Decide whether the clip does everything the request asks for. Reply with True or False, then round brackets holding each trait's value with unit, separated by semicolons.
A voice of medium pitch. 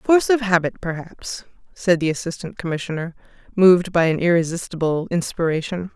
True (175 Hz)